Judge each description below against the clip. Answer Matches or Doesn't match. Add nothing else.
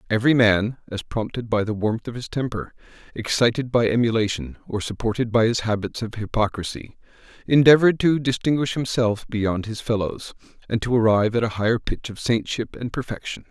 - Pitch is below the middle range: Matches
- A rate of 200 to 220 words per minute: Doesn't match